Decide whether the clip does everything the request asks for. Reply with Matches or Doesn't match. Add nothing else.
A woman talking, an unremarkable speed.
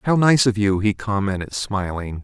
Doesn't match